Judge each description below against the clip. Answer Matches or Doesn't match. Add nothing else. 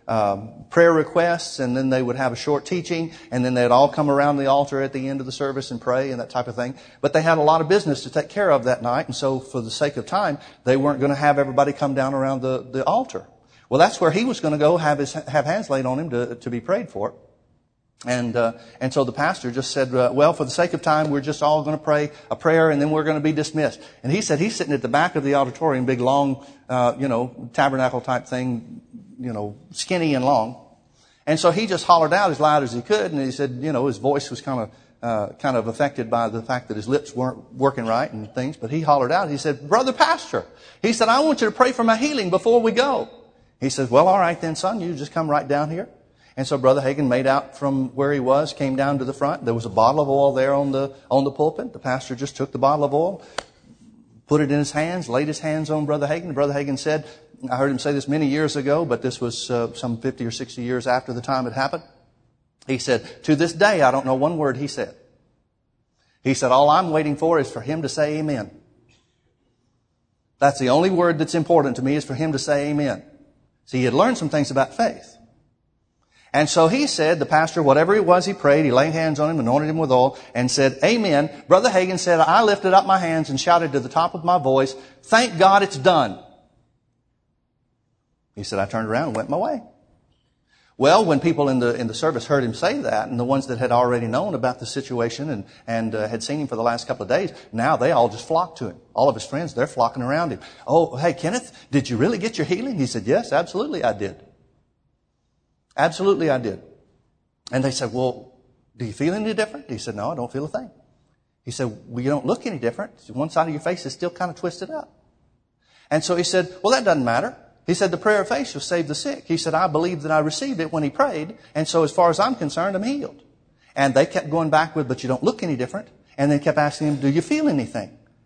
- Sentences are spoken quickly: Matches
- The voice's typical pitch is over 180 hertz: Doesn't match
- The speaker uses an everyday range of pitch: Matches